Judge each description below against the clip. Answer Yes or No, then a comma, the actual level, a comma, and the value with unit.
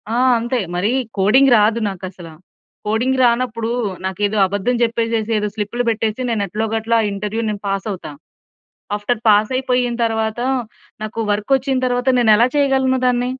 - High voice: Yes, high, 225 Hz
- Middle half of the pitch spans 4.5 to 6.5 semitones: No, average, 2.8 semitones